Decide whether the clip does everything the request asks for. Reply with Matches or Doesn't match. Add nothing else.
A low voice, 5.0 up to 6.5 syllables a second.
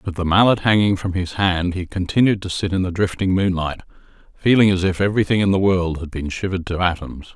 Matches